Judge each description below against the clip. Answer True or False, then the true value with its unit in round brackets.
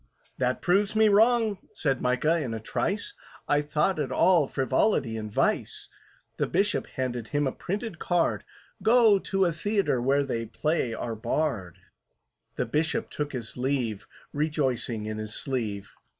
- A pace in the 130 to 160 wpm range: True (150 wpm)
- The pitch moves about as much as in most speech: False (7.5 semitones)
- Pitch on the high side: False (145 Hz)